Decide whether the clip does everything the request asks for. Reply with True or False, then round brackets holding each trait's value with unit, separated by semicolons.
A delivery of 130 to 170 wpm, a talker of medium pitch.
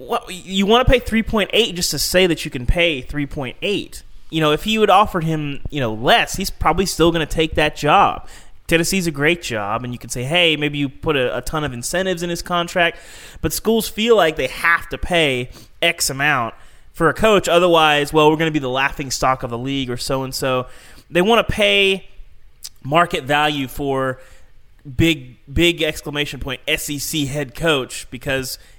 False (200 wpm; 150 Hz)